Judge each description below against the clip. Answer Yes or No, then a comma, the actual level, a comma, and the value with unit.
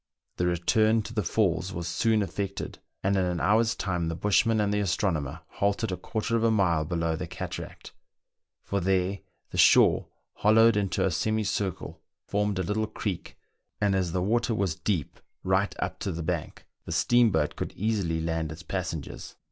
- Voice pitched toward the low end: Yes, very low, 95 Hz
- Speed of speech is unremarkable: Yes, average, 180 wpm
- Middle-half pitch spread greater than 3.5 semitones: Yes, average, 3.9 semitones